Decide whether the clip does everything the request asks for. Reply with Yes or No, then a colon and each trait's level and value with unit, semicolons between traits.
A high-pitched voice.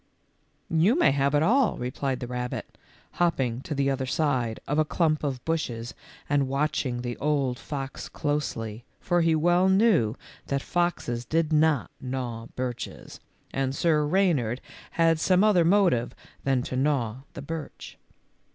No: medium, 140 Hz